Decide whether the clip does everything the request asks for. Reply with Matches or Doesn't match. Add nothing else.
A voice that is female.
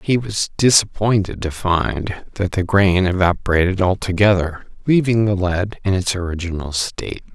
Doesn't match